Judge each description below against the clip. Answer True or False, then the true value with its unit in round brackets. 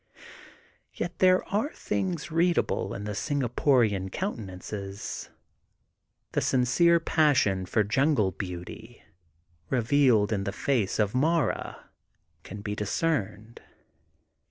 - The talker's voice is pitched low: True (120 Hz)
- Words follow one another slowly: True (105 wpm)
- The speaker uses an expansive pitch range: True (7.3 semitones)